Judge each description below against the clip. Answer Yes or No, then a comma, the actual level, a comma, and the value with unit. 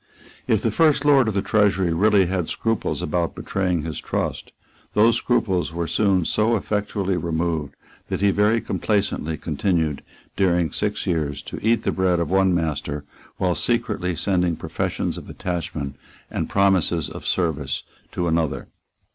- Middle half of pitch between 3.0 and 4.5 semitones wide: Yes, average, 3.9 semitones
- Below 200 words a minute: Yes, average, 150 wpm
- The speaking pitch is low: Yes, very low, 90 Hz